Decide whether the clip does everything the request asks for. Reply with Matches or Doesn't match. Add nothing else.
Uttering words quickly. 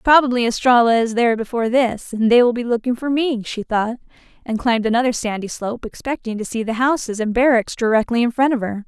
Matches